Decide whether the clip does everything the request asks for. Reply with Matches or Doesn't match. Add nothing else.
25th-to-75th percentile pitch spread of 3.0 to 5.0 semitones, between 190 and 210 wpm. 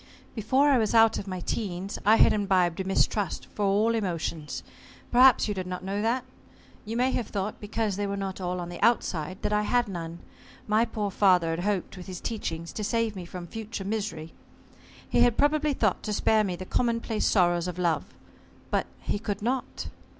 Matches